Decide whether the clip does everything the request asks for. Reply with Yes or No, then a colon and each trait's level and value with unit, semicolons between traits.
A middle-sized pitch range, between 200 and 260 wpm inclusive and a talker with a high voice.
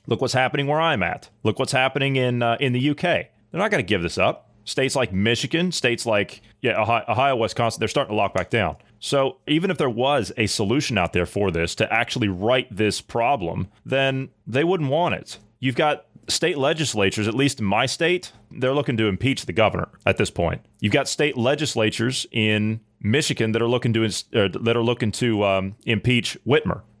No: average, 3.8 semitones; fast, 205 wpm; low, 115 Hz